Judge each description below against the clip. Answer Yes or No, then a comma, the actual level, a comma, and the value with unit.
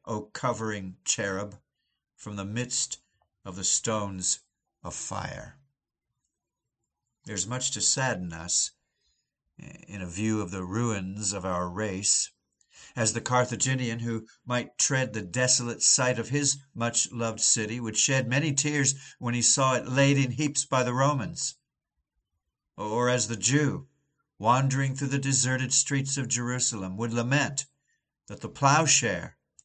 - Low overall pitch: Yes, low, 120 Hz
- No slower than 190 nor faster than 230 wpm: No, average, 140 wpm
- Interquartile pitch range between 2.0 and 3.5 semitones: No, average, 4.3 semitones